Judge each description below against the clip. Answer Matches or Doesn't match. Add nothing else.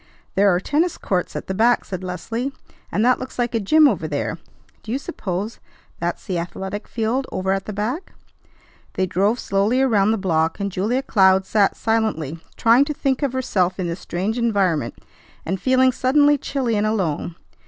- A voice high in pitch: Matches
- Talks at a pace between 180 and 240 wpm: Matches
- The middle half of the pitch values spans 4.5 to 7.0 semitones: Matches